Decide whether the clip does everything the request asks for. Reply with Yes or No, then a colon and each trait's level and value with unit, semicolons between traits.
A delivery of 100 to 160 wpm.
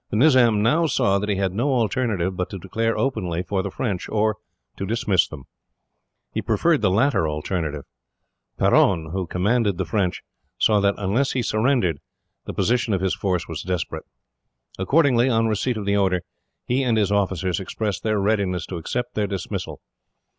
No: average, 175 wpm